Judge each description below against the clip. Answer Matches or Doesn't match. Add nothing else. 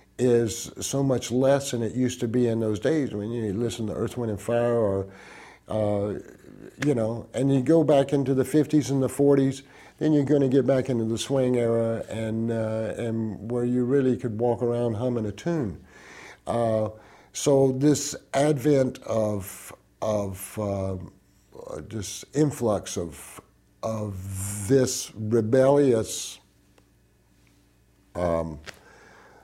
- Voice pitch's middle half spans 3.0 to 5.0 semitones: Matches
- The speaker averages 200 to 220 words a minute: Doesn't match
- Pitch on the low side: Matches